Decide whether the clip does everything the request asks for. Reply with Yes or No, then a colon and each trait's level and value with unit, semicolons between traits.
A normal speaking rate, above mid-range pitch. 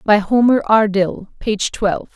Yes: average, 165 wpm; high, 210 Hz